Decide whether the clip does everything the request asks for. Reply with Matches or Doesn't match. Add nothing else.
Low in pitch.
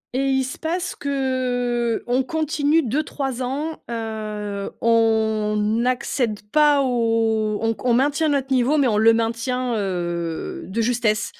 Doesn't match